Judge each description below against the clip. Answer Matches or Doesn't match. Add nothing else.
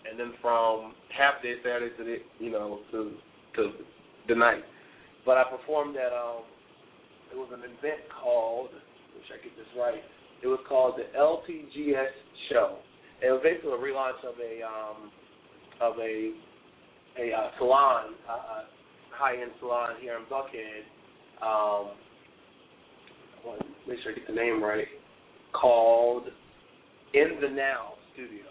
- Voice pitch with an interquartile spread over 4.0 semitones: Doesn't match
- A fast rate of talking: Doesn't match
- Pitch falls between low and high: Doesn't match